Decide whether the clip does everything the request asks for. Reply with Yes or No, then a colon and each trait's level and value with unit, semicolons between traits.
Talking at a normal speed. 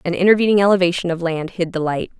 No: fast, 220 wpm